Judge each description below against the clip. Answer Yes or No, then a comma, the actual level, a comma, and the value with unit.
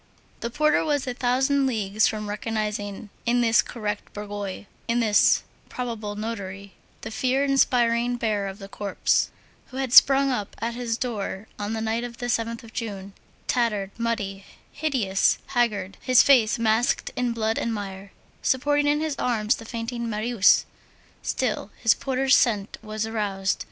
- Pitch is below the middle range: No, high, 230 Hz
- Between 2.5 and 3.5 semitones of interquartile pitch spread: Yes, average, 2.9 semitones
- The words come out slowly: No, average, 155 wpm